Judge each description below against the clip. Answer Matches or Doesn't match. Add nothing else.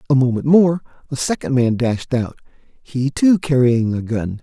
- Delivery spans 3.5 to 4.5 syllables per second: Matches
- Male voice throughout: Matches